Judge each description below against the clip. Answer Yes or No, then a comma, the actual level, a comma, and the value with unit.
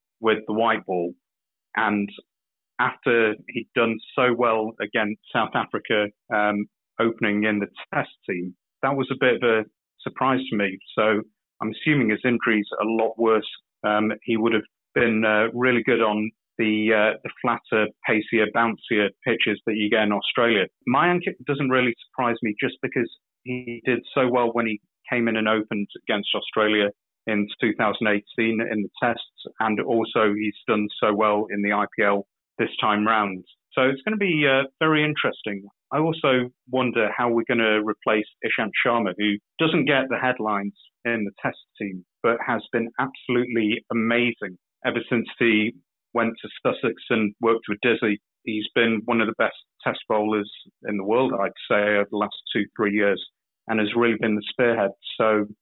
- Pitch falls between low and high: No, low, 110 Hz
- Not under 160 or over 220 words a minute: Yes, average, 175 wpm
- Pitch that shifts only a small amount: Yes, narrow, 2.2 semitones